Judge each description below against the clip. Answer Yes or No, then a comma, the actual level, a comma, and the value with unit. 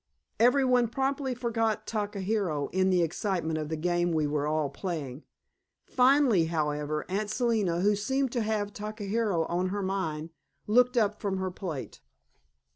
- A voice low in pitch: No, high, 195 Hz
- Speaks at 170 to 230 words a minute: No, average, 150 wpm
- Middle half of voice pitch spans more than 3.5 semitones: Yes, wide, 5.5 semitones